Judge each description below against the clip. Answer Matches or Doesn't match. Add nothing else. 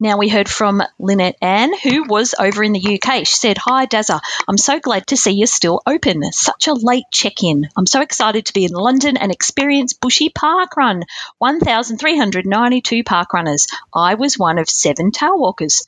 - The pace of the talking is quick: Doesn't match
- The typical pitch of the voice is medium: Doesn't match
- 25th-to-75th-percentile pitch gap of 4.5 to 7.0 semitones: Matches